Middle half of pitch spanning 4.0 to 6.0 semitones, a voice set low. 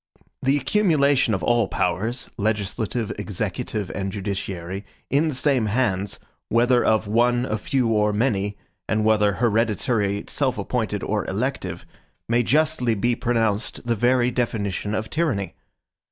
No: average, 3.2 semitones; low, 110 Hz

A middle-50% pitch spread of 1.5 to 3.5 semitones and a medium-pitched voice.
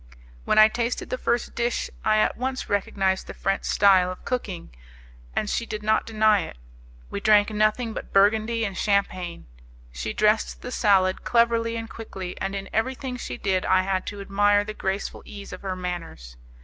No: average, 2.9 semitones; high, 205 Hz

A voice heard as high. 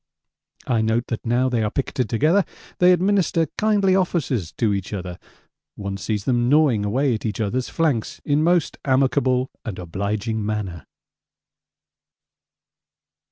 No: low, 120 Hz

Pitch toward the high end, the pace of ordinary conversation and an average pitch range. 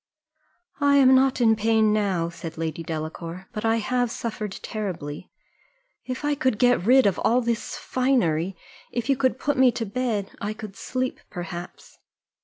No: high, 220 Hz; average, 165 wpm; wide, 5.9 semitones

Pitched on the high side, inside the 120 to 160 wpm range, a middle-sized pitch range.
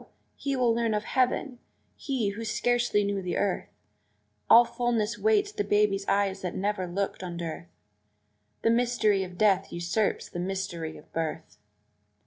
Yes: high, 205 Hz; average, 150 wpm; average, 4.1 semitones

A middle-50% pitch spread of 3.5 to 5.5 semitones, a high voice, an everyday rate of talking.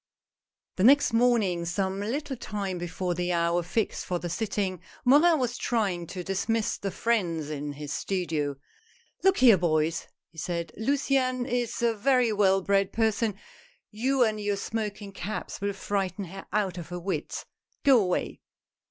Yes: average, 4.7 semitones; high, 200 Hz; average, 165 wpm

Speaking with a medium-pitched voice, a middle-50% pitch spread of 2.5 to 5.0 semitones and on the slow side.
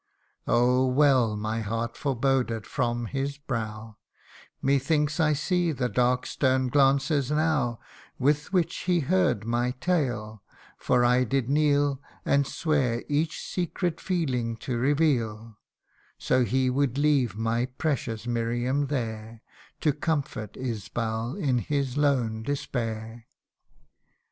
No: low, 130 Hz; average, 3.9 semitones; slow, 120 wpm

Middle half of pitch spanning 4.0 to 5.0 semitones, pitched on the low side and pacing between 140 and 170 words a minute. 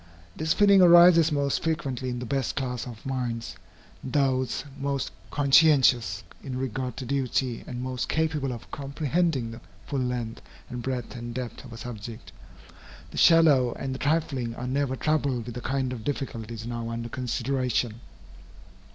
No: average, 2.9 semitones; low, 130 Hz; average, 155 wpm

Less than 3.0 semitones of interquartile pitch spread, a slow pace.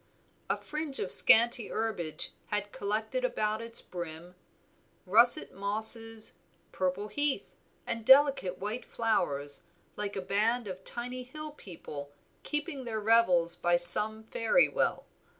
No: average, 4.3 semitones; slow, 125 wpm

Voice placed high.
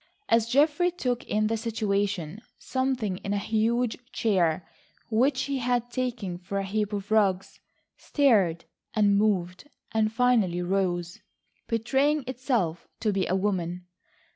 Yes: high, 215 Hz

